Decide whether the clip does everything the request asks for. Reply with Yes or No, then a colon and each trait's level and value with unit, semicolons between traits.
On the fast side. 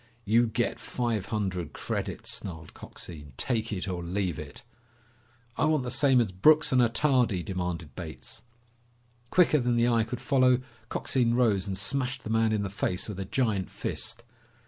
No: average, 170 wpm